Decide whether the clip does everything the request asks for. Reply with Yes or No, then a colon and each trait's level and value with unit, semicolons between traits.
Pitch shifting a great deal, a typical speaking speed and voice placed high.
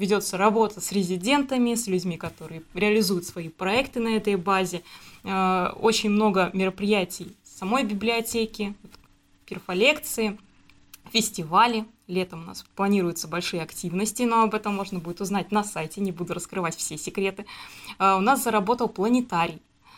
No: average, 3.7 semitones; average, 130 wpm; high, 200 Hz